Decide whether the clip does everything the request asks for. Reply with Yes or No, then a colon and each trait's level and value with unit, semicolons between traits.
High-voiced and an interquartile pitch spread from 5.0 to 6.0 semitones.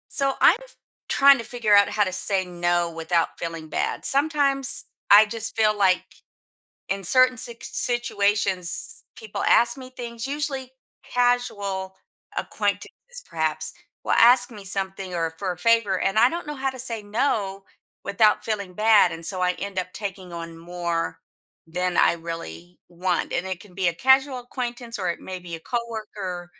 Yes: high, 200 Hz; wide, 5.4 semitones